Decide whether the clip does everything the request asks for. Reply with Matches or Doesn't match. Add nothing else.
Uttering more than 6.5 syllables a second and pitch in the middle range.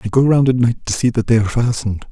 Doesn't match